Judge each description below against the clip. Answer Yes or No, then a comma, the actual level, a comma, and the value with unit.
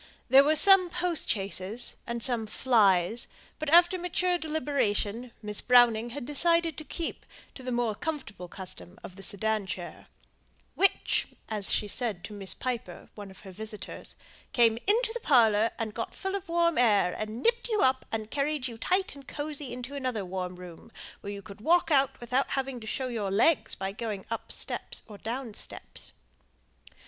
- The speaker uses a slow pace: No, average, 175 wpm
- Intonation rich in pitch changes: Yes, wide, 6.3 semitones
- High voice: Yes, high, 240 Hz